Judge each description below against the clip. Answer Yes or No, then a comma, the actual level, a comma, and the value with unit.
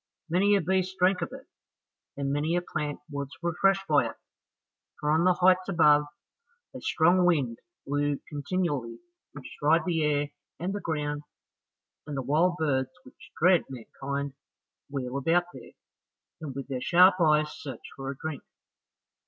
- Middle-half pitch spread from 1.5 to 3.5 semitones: No, average, 4.0 semitones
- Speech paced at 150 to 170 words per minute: Yes, average, 155 wpm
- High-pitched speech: No, medium, 150 Hz